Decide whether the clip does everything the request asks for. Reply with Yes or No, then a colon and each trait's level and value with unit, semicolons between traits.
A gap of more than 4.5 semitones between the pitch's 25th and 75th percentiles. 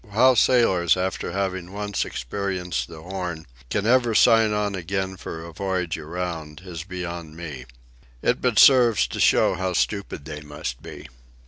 No: average, 3.7 semitones